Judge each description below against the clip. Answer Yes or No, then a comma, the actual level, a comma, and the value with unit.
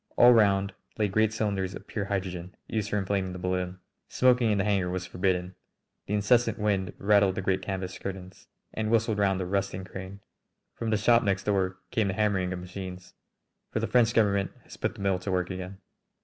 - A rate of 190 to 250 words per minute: Yes, average, 200 wpm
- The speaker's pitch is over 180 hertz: No, low, 100 Hz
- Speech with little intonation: Yes, narrow, 2.2 semitones